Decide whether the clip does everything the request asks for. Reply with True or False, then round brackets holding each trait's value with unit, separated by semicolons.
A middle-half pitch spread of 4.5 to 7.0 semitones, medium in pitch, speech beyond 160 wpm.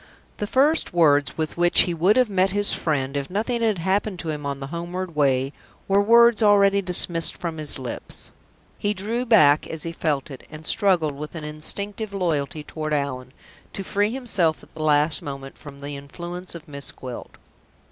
True (5.4 semitones; 165 Hz; 190 wpm)